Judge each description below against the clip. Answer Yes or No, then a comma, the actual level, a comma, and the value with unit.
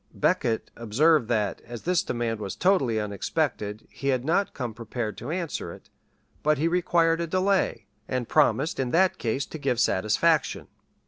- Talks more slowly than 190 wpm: Yes, average, 170 wpm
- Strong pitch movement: Yes, wide, 6.5 semitones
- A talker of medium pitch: No, low, 130 Hz